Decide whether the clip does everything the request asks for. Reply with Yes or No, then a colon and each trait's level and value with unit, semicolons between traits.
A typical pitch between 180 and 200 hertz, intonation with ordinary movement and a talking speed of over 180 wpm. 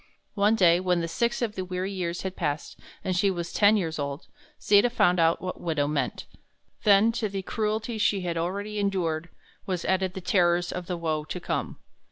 Yes: medium, 185 Hz; average, 3.1 semitones; average, 195 wpm